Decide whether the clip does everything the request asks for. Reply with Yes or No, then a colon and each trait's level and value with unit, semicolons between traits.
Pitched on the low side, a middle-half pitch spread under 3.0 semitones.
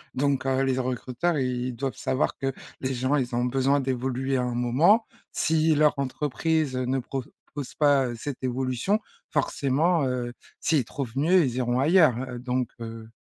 Yes: low, 130 Hz; narrow, 2.5 semitones